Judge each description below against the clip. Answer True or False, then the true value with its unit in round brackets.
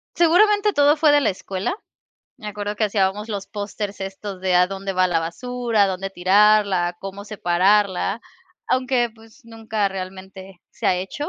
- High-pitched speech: True (200 Hz)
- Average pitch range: True (3.0 semitones)